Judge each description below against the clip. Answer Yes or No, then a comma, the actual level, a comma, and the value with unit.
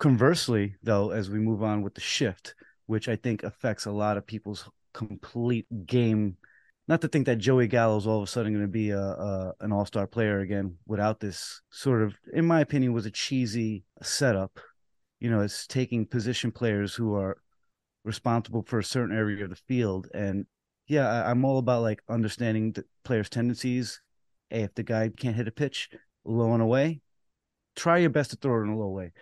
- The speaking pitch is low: Yes, low, 110 Hz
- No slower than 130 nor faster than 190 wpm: No, fast, 205 wpm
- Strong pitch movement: No, average, 3.0 semitones